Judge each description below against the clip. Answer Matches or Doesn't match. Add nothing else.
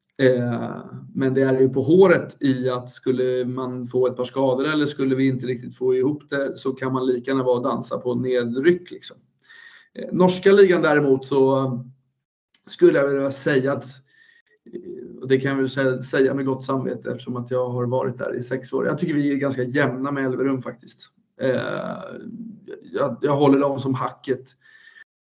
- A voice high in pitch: Doesn't match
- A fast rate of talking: Doesn't match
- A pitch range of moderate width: Doesn't match